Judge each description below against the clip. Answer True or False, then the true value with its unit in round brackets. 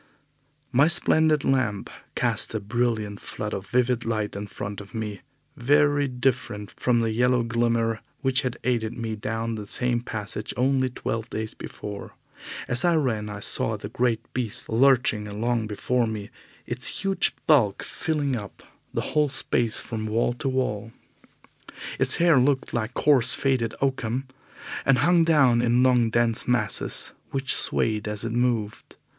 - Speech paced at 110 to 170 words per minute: True (155 wpm)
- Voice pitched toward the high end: False (120 Hz)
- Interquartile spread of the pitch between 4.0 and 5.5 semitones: False (3.2 semitones)